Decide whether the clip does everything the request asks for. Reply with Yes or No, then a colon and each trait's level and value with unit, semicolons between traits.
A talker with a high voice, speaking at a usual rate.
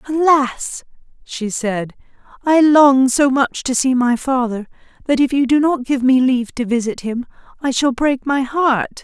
Yes: very high, 260 Hz; average, 180 wpm